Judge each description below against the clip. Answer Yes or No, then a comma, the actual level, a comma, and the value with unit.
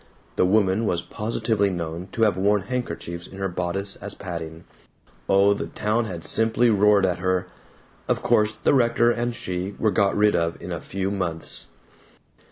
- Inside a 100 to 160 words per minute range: No, average, 175 wpm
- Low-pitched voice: Yes, low, 100 Hz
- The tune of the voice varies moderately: Yes, average, 3.3 semitones